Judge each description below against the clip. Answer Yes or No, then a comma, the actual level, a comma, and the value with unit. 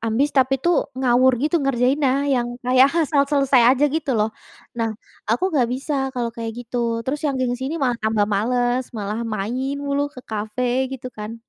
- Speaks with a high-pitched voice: Yes, very high, 255 Hz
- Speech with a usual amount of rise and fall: Yes, average, 3.0 semitones